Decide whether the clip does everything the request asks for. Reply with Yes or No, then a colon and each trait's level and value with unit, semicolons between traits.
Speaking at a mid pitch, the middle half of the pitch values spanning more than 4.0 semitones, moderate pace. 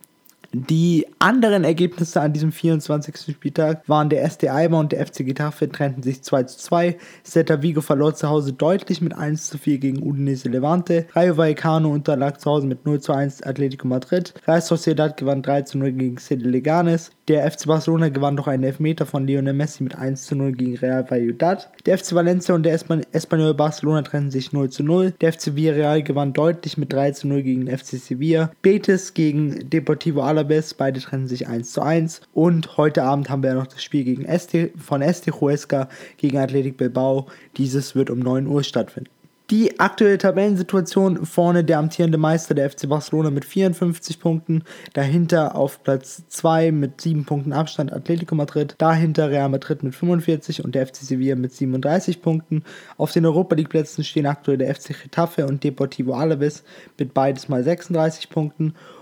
No: medium, 155 Hz; average, 3.0 semitones; average, 180 wpm